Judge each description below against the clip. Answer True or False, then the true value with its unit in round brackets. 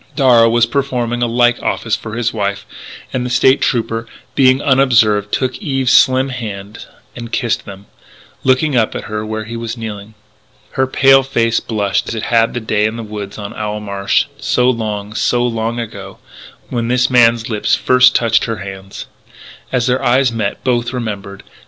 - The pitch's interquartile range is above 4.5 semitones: False (2.8 semitones)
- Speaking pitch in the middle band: False (115 Hz)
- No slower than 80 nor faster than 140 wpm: False (175 wpm)